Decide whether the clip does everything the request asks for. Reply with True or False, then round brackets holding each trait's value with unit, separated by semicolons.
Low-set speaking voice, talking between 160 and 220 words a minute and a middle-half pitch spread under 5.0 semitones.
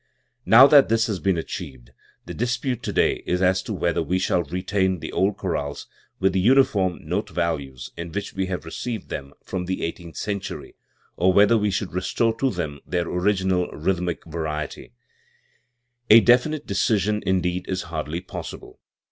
True (95 Hz; 165 wpm; 3.5 semitones)